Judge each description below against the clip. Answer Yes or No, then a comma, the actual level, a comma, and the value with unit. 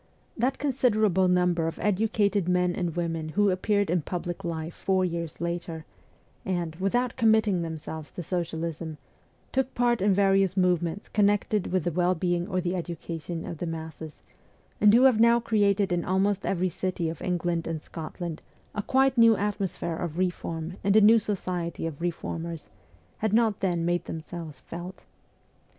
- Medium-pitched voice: Yes, medium, 180 Hz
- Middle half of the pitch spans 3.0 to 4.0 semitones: Yes, average, 3.4 semitones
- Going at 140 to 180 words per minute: Yes, average, 160 wpm